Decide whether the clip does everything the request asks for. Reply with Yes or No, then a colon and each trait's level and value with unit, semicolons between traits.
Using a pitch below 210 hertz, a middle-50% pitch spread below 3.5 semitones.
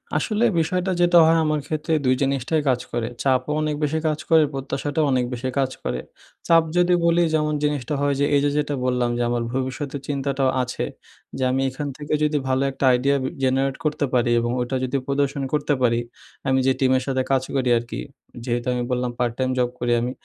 Yes: low, 135 Hz; average, 2.8 semitones